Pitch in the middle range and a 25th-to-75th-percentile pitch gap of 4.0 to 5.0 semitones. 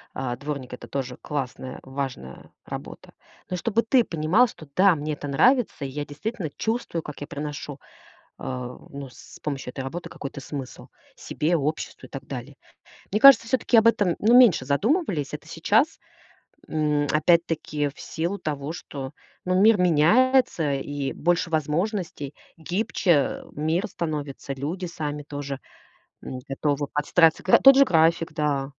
Yes: medium, 155 Hz; average, 4.5 semitones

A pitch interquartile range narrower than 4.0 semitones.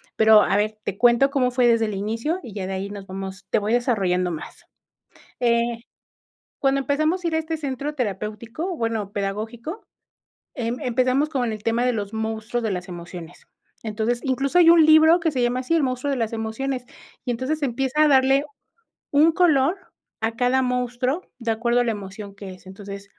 No: average, 4.4 semitones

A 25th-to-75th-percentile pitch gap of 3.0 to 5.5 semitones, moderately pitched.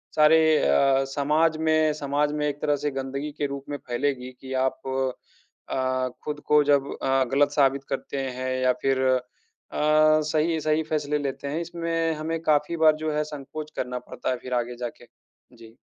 No: narrow, 2.5 semitones; medium, 145 Hz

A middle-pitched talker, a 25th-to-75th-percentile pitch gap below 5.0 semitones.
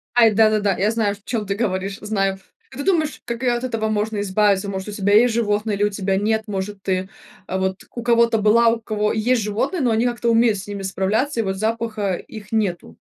No: high, 215 Hz; narrow, 2.6 semitones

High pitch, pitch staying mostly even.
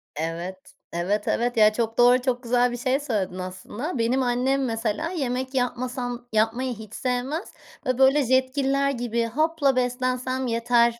Yes: high, 245 Hz; narrow, 2.3 semitones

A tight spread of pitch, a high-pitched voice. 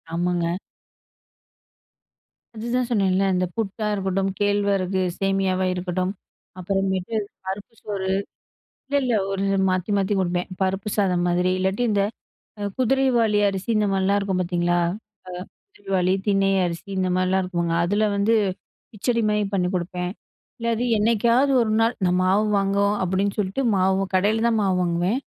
Yes: narrow, 2.3 semitones; high, 195 Hz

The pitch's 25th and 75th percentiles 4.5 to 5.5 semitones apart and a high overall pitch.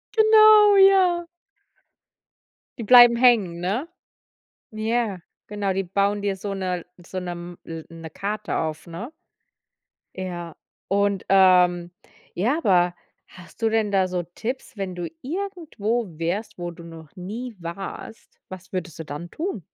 Yes: average, 5.1 semitones; high, 195 Hz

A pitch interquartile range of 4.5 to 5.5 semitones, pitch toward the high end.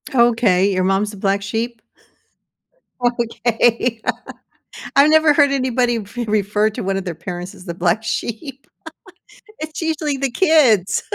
Yes: average, 5.0 semitones; high, 225 Hz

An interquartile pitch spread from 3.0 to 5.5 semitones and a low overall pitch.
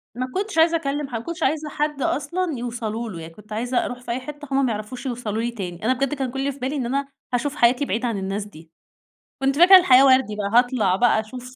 No: average, 4.0 semitones; very high, 250 Hz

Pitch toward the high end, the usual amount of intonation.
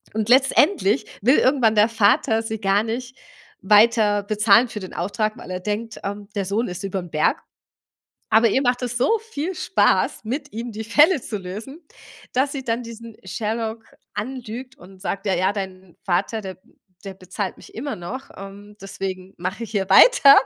Yes: high, 215 Hz; average, 3.8 semitones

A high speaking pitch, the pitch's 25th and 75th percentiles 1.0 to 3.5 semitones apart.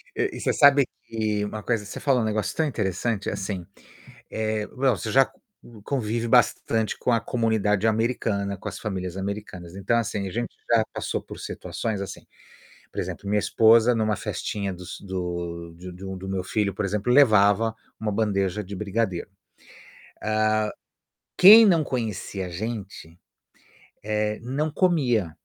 No: low, 105 Hz; average, 3.0 semitones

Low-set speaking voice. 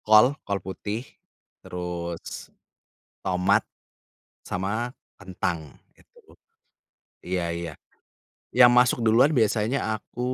Yes: low, 100 Hz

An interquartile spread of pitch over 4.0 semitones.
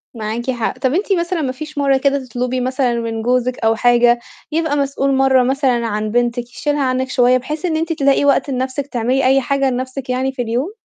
No: narrow, 2.4 semitones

